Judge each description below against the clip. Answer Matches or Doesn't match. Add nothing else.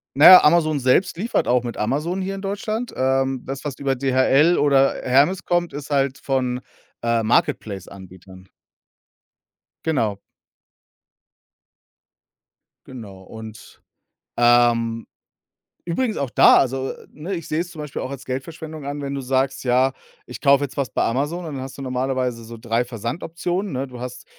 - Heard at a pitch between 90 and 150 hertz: Matches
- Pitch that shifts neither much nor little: Matches